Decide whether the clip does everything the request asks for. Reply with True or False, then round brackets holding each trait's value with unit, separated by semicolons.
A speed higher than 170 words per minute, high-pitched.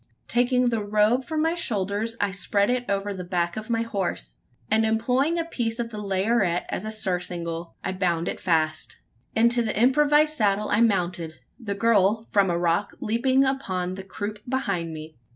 True (180 wpm; 210 Hz)